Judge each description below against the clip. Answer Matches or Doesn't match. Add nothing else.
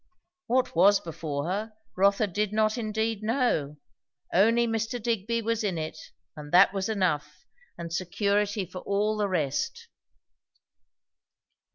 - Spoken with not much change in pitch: Doesn't match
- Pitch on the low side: Doesn't match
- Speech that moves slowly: Matches